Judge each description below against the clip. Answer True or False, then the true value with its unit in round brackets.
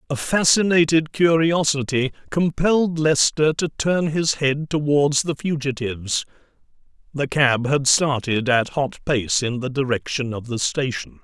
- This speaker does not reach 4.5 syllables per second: True (4.3 syllables/s)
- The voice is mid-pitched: True (145 Hz)